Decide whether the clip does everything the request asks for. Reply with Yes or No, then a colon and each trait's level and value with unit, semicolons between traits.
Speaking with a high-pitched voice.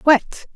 Yes: very high, 290 Hz